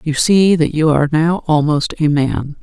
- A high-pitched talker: No, medium, 155 Hz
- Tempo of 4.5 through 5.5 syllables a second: Yes, 4.6 syllables/s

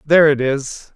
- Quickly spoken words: No, average, 190 wpm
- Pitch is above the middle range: No, medium, 145 Hz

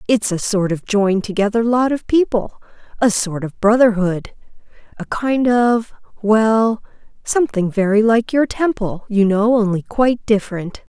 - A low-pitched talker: No, high, 215 Hz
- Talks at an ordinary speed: No, slow, 130 wpm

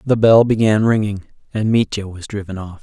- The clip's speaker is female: No, male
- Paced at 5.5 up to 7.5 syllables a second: No, 5.2 syllables/s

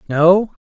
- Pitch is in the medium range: Yes, medium, 175 Hz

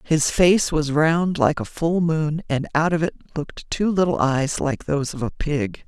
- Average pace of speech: No, fast, 215 wpm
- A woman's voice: Yes, female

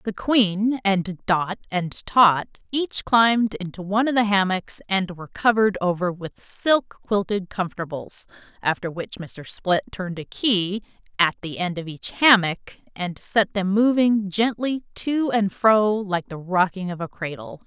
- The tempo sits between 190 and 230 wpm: No, average, 165 wpm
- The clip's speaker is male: No, female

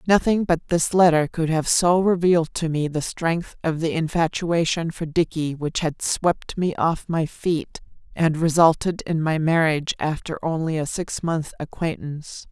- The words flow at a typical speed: Yes, average, 170 wpm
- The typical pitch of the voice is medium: Yes, medium, 165 Hz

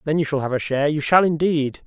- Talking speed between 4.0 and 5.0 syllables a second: No, 6.3 syllables/s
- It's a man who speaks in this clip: Yes, male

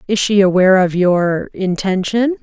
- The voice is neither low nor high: No, high, 195 Hz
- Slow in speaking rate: Yes, slow, 125 wpm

